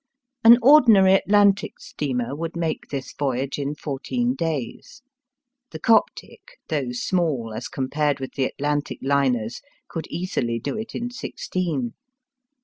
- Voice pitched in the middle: Yes, medium, 150 Hz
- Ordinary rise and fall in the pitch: No, wide, 6.3 semitones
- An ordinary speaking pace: No, slow, 130 wpm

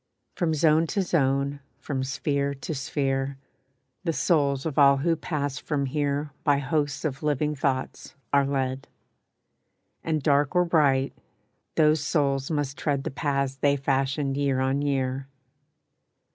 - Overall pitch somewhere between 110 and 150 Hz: Yes, medium, 140 Hz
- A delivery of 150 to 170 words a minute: No, average, 140 wpm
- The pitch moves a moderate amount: No, narrow, 1.9 semitones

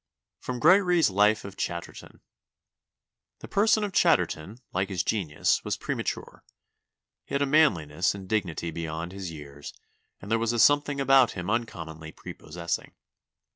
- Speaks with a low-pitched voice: Yes, low, 100 Hz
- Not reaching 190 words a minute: Yes, average, 145 wpm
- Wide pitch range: Yes, wide, 8.2 semitones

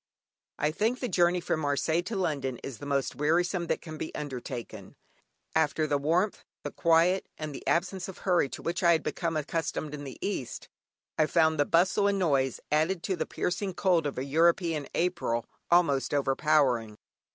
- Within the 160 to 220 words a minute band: Yes, average, 180 wpm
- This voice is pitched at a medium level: Yes, medium, 160 Hz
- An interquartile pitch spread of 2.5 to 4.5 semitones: Yes, average, 3.7 semitones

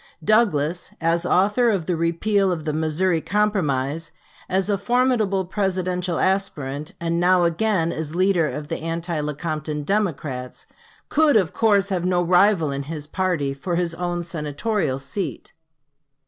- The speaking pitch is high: No, medium, 175 Hz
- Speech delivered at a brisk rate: No, average, 145 wpm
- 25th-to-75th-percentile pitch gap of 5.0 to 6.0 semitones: No, average, 4.0 semitones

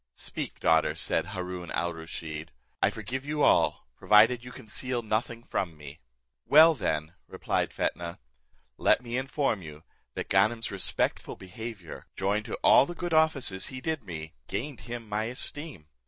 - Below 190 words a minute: Yes, average, 155 wpm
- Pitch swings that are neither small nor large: No, wide, 6.9 semitones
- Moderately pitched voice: No, low, 110 Hz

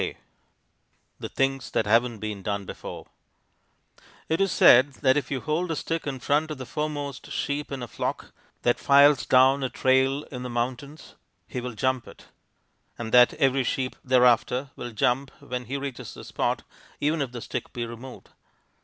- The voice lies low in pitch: Yes, low, 130 Hz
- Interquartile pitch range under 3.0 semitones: Yes, narrow, 2.5 semitones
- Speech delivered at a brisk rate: No, average, 180 wpm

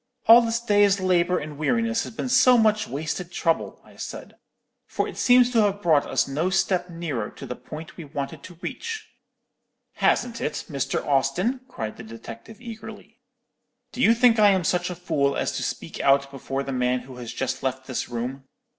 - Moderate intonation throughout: No, wide, 8.3 semitones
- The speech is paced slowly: No, average, 190 wpm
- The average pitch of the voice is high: No, medium, 175 Hz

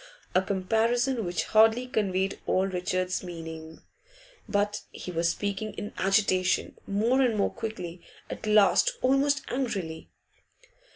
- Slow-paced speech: Yes, slow, 120 wpm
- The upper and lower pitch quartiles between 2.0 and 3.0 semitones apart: No, average, 3.6 semitones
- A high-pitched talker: Yes, high, 200 Hz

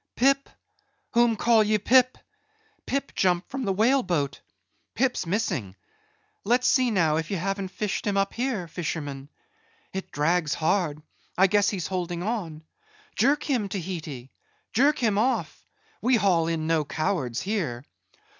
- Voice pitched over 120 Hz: Yes, high, 190 Hz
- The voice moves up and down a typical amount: No, wide, 6.2 semitones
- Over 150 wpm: No, average, 145 wpm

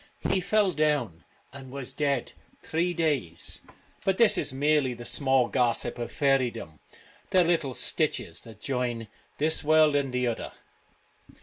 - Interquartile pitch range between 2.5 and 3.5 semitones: No, average, 4.3 semitones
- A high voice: No, low, 135 Hz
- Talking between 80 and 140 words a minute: No, average, 150 wpm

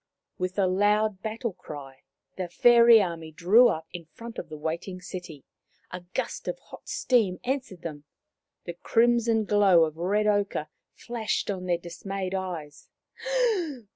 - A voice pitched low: No, medium, 185 Hz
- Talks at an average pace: Yes, average, 145 wpm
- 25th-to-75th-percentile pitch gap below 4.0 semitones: No, average, 4.4 semitones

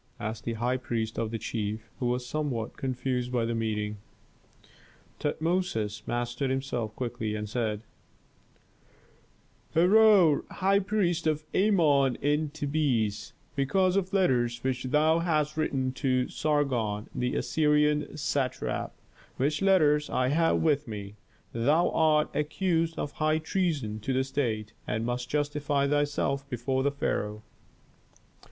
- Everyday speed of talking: No, slow, 130 wpm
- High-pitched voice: No, low, 135 Hz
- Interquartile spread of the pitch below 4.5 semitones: No, average, 4.8 semitones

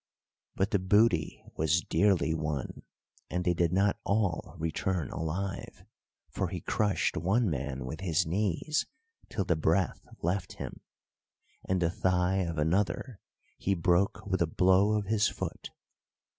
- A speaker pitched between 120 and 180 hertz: No, very low, 90 Hz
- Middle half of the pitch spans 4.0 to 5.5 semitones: No, average, 3.2 semitones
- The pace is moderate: Yes, average, 145 wpm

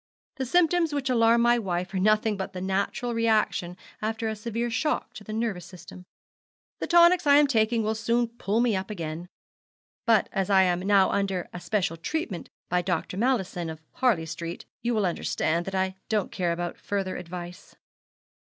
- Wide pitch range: No, average, 4.4 semitones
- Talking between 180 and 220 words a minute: Yes, average, 185 wpm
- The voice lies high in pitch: Yes, high, 205 Hz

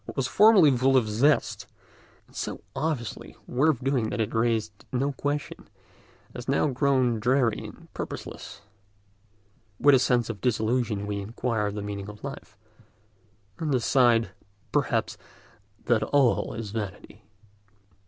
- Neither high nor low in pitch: No, low, 120 Hz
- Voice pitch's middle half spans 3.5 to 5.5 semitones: Yes, average, 3.8 semitones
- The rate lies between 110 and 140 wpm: Yes, slow, 135 wpm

